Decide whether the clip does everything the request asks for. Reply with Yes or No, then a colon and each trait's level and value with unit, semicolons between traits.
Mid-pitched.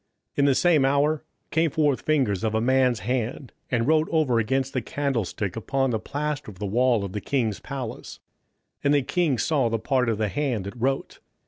No: low, 130 Hz